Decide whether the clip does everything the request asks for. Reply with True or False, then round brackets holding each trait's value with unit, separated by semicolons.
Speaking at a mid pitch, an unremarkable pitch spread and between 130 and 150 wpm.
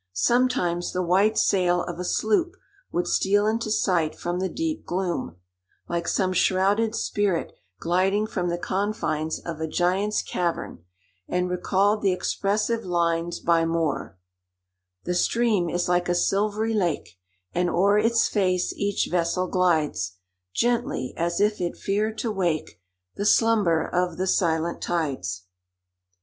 True (180 Hz; 3.3 semitones; 140 wpm)